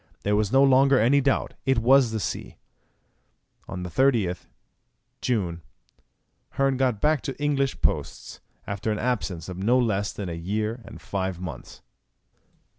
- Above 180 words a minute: No, average, 155 wpm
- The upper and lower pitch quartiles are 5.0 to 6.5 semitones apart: Yes, wide, 5.5 semitones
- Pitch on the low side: Yes, low, 110 Hz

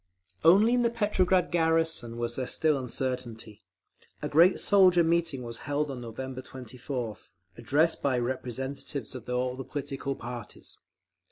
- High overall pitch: No, low, 135 Hz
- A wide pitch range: No, average, 4.7 semitones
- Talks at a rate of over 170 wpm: No, average, 140 wpm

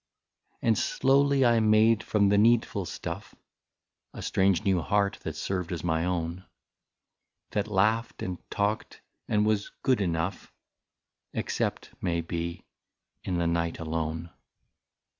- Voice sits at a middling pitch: No, very low, 95 Hz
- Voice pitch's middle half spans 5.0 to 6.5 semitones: No, average, 4.3 semitones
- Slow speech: Yes, slow, 130 wpm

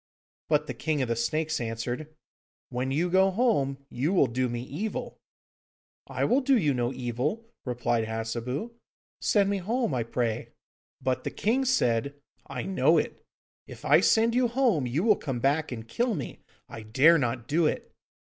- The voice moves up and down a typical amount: No, wide, 8.6 semitones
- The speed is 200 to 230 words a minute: No, average, 175 wpm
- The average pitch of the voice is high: No, medium, 140 Hz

